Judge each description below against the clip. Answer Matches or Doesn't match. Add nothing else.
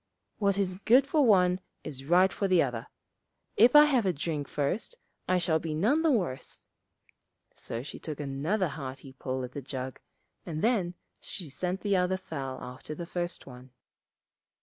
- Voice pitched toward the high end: Doesn't match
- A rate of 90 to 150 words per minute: Doesn't match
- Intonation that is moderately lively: Doesn't match